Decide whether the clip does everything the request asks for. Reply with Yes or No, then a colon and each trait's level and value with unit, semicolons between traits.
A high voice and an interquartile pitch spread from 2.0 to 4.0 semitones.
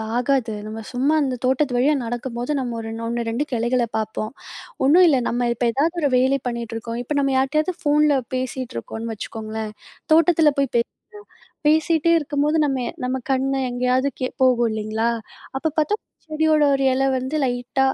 Yes: very high, 260 Hz; average, 3.5 semitones